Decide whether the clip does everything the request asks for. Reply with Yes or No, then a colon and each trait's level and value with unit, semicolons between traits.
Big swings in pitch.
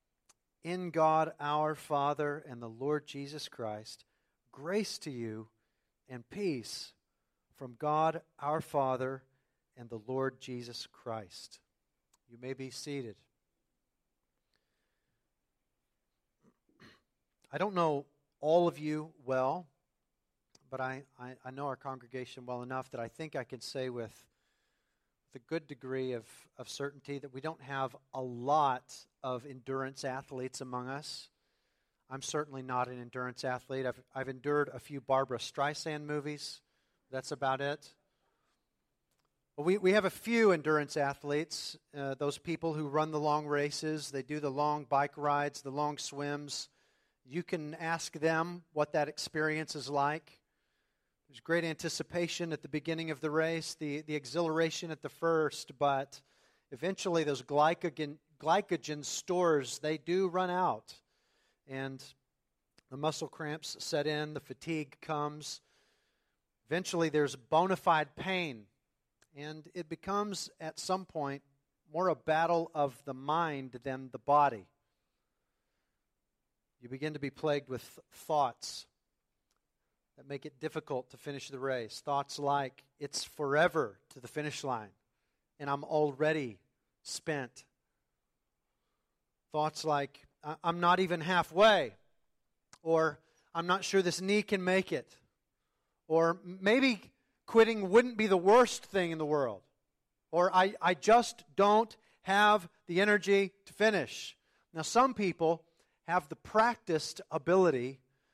No: average, 3.7 semitones